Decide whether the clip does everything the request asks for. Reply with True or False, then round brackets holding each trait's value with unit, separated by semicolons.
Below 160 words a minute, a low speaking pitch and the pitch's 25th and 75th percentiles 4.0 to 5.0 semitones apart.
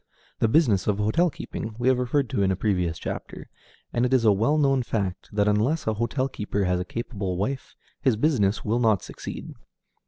False (205 wpm; 110 Hz; 4.5 semitones)